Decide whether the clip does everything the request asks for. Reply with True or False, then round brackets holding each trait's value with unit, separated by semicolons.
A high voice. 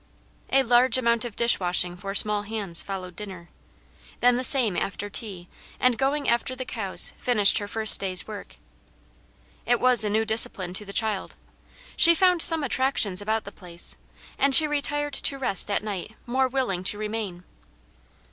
True (220 Hz)